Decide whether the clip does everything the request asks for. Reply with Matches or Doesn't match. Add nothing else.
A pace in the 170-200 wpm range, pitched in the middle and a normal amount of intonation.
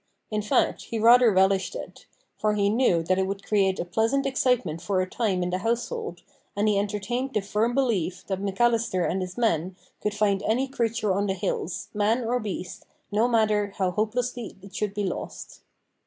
Doesn't match